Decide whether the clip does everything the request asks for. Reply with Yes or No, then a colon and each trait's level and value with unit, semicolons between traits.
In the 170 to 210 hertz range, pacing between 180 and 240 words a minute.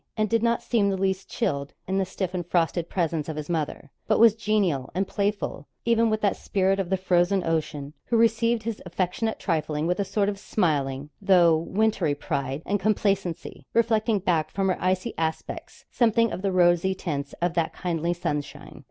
Yes: medium, 185 Hz; average, 185 wpm